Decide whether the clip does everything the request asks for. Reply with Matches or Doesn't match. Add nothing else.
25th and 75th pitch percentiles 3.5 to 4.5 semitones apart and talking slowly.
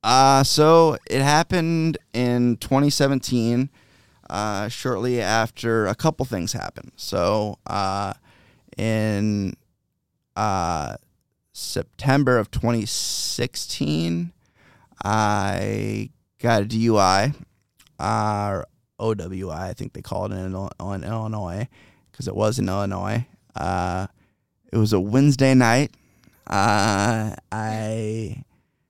Matches